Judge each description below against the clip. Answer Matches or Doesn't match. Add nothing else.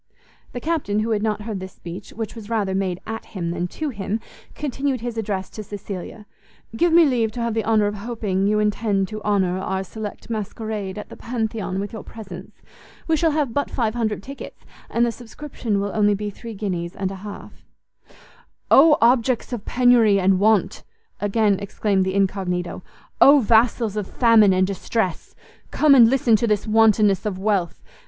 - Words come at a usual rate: Matches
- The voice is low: Doesn't match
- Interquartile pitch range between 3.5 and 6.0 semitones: Doesn't match